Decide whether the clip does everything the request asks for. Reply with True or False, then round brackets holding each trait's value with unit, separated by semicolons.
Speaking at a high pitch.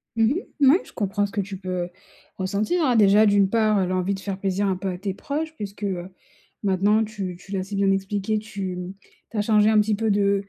True (200 Hz)